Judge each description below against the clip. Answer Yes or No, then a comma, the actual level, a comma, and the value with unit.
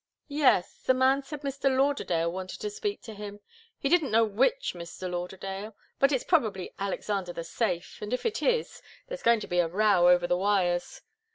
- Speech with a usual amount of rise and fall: No, wide, 7.3 semitones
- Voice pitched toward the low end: No, high, 210 Hz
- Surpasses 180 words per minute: Yes, average, 190 wpm